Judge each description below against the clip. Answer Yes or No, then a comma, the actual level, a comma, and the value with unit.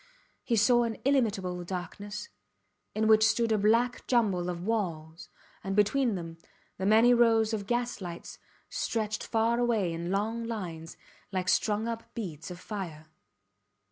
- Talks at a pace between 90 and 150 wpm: Yes, average, 140 wpm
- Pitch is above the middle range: Yes, high, 210 Hz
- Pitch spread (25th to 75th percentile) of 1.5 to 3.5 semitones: No, average, 4.3 semitones